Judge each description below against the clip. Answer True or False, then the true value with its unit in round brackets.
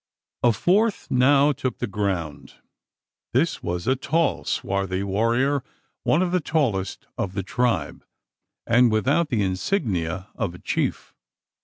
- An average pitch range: False (6.8 semitones)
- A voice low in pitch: True (115 Hz)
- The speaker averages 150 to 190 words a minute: False (135 wpm)